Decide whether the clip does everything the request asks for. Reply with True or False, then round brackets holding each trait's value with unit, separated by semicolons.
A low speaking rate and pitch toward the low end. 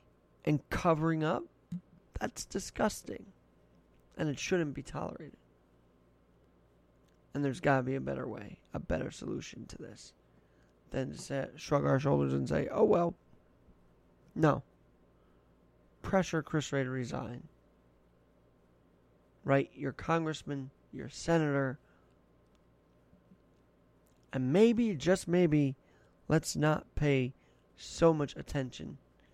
True (110 wpm; 130 Hz)